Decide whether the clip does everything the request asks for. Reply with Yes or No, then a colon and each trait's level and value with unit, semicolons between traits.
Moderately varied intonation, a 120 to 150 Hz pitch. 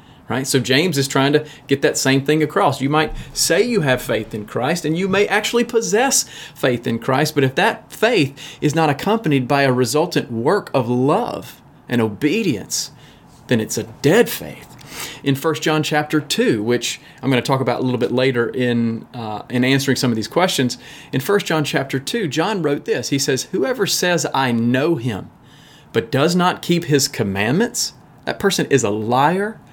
Yes: average, 3.9 semitones; medium, 140 Hz